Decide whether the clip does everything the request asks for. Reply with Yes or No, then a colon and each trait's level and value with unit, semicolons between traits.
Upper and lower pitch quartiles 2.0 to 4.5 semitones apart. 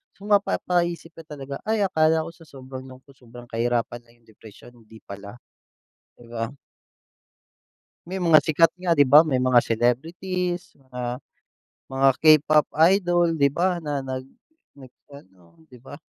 No: average, 5.3 semitones